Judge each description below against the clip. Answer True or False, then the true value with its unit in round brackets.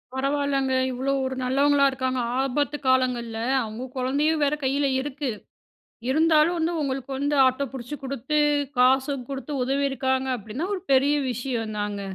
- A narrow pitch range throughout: True (2.0 semitones)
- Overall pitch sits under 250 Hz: False (270 Hz)